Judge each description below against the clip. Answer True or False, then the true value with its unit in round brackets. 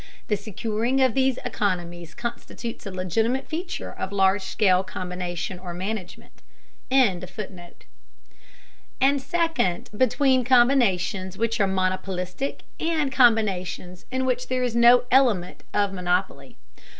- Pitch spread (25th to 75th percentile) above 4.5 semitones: True (5.6 semitones)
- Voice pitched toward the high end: True (210 Hz)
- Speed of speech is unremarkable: False (115 wpm)